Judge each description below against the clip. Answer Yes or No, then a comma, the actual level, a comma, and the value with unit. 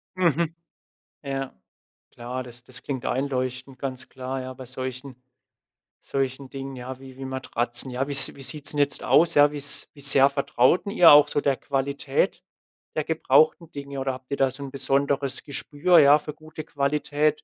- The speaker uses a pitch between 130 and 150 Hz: Yes, low, 135 Hz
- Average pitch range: No, narrow, 1.9 semitones